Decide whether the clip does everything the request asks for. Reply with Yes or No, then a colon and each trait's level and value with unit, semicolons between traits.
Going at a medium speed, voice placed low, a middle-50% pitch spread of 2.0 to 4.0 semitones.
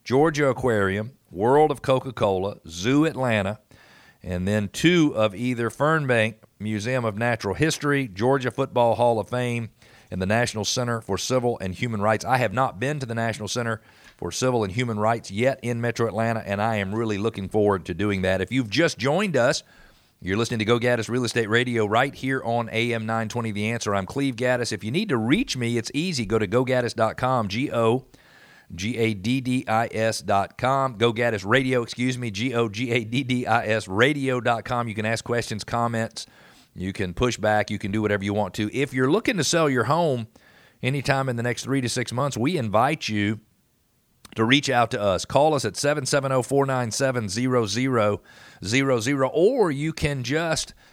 Yes: average, 180 wpm; low, 120 Hz; average, 3.1 semitones